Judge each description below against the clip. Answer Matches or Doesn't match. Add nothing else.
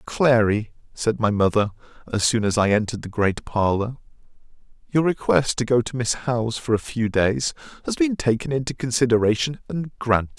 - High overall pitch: Doesn't match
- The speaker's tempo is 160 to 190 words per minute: Matches